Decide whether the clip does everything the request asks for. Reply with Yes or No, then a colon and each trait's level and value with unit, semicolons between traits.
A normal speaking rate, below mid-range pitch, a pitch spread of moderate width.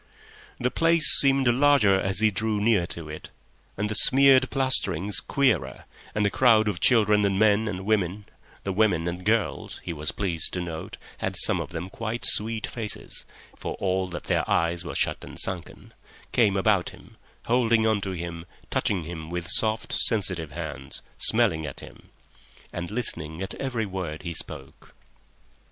Yes: average, 170 wpm; low, 100 Hz; average, 4.4 semitones